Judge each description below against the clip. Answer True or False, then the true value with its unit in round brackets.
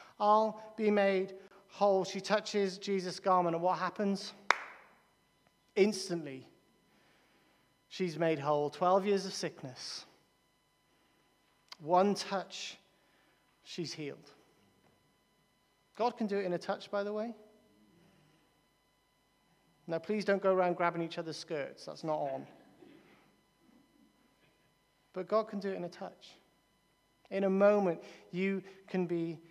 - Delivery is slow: True (120 wpm)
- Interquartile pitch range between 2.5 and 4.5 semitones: True (2.8 semitones)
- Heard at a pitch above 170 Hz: True (190 Hz)